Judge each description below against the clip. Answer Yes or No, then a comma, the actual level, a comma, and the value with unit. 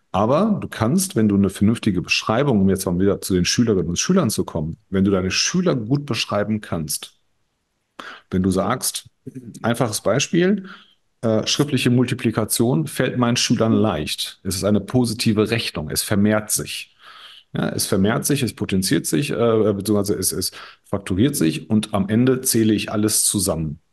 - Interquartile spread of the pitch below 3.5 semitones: No, average, 4.0 semitones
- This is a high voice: No, low, 110 Hz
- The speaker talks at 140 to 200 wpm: Yes, average, 165 wpm